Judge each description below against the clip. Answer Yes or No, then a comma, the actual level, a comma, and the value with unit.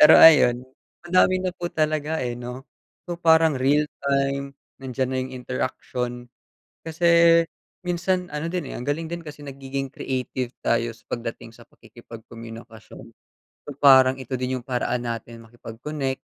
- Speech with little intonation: No, average, 3.9 semitones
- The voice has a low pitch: Yes, low, 130 Hz